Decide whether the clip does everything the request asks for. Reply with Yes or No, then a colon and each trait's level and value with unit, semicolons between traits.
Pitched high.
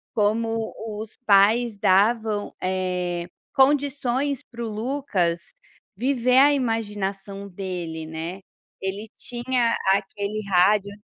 Yes: high, 210 Hz